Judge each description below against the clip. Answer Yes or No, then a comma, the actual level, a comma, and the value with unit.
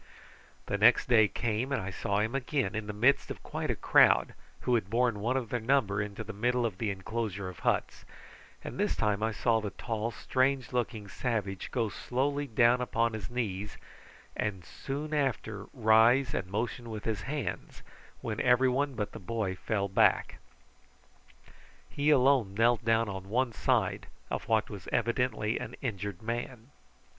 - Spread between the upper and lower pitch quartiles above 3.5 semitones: No, average, 3.2 semitones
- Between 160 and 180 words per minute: Yes, average, 170 wpm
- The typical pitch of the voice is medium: No, low, 115 Hz